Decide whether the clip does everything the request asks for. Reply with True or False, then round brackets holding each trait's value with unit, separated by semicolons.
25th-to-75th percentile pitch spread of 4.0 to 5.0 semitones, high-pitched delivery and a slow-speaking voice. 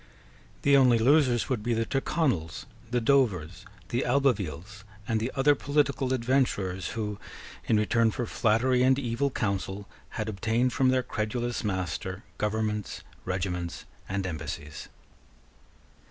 False (4.6 semitones; 115 Hz; 125 wpm)